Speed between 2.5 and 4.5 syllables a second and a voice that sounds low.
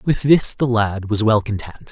Yes: 4.3 syllables/s; low, 110 Hz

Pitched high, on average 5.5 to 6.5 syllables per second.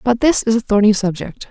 Yes: high, 220 Hz; 5.8 syllables/s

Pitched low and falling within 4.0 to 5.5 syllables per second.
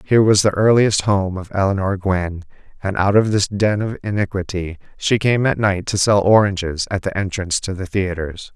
Yes: low, 100 Hz; 5.2 syllables/s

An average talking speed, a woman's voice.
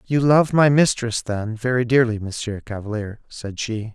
No: average, 165 wpm; male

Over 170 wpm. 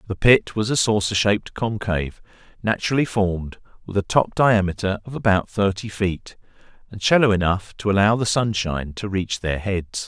No: average, 165 wpm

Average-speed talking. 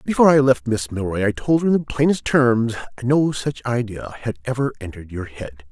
No: fast, 210 wpm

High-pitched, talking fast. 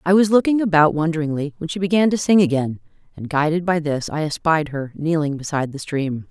No: medium, 160 Hz; fast, 210 wpm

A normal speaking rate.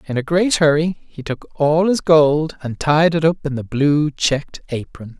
No: fast, 210 wpm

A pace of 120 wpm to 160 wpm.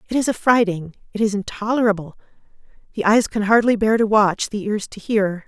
No: average, 185 wpm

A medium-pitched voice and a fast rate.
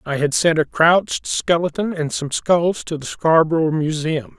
No: medium, 160 Hz; average, 180 wpm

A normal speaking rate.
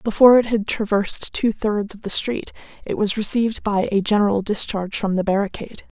Yes: average, 190 wpm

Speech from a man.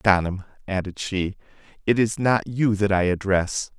Yes: male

